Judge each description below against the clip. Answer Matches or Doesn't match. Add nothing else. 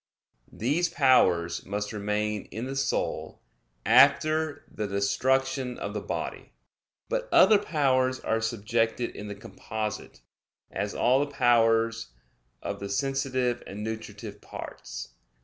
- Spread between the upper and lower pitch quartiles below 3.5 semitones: Doesn't match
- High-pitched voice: Doesn't match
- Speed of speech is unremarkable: Doesn't match